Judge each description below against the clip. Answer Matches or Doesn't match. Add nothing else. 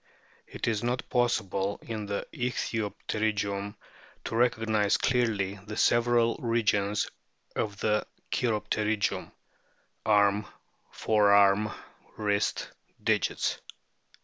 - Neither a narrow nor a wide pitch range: Doesn't match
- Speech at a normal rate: Doesn't match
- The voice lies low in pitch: Matches